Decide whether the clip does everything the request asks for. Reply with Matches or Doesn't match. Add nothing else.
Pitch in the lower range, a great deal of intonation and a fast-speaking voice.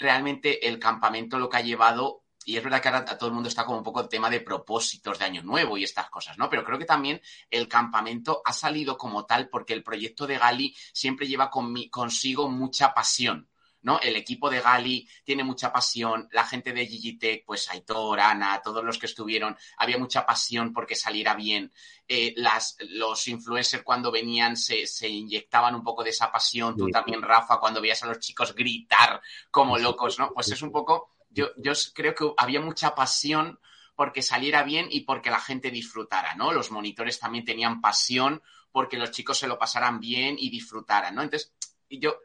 Doesn't match